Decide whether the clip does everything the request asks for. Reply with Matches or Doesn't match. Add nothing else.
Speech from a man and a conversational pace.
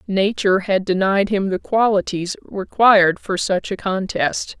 Doesn't match